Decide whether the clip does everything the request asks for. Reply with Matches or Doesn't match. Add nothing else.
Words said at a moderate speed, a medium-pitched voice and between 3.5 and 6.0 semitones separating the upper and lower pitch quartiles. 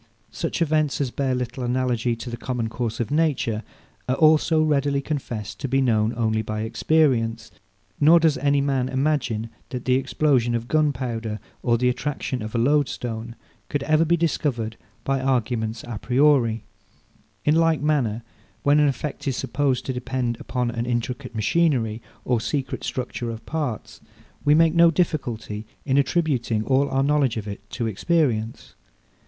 Doesn't match